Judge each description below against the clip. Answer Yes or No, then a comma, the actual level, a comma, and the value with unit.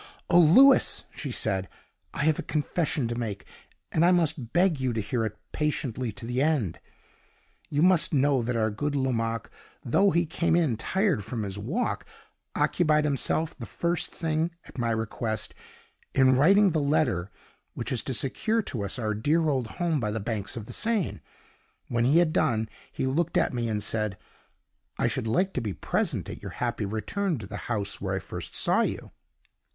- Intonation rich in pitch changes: Yes, wide, 6.5 semitones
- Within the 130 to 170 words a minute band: No, average, 190 wpm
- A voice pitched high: No, low, 130 Hz